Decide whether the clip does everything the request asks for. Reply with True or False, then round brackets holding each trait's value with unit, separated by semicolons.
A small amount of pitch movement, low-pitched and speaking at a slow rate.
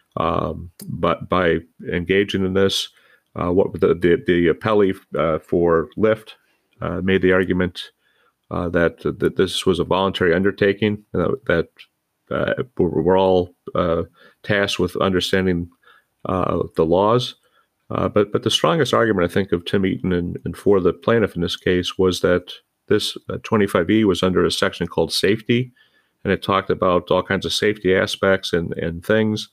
False (2.2 semitones; 95 Hz; 170 wpm)